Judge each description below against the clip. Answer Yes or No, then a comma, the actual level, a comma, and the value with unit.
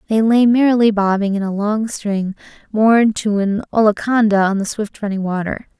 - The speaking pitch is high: Yes, high, 210 Hz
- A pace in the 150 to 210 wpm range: Yes, average, 175 wpm